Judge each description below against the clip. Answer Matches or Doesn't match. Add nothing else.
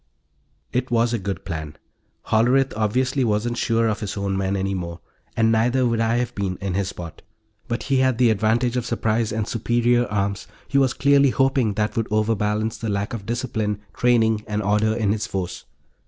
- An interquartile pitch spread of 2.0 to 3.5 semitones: Matches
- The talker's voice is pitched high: Doesn't match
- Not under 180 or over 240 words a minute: Matches